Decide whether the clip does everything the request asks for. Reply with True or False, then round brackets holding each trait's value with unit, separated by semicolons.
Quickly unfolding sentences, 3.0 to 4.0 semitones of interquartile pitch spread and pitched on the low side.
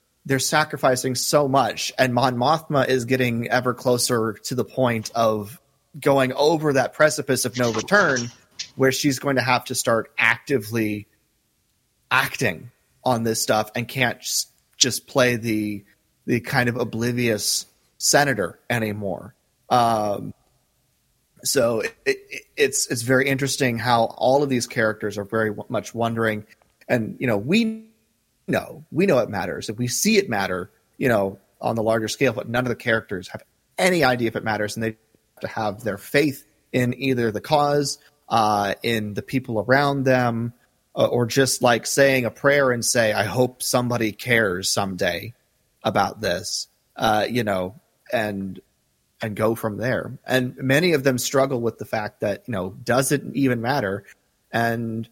False (165 wpm; 3.3 semitones; 120 Hz)